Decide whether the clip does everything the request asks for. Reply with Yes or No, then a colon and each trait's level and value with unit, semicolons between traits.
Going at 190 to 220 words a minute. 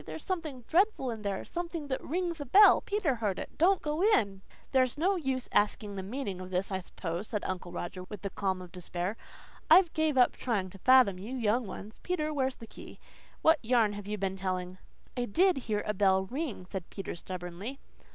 Yes: fast, 205 wpm